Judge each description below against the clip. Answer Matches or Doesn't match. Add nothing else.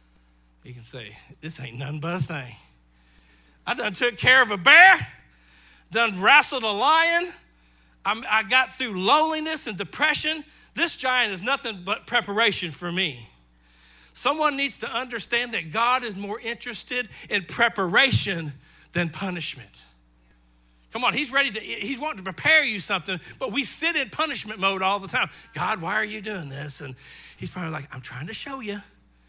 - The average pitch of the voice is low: Doesn't match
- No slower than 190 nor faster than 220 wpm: Doesn't match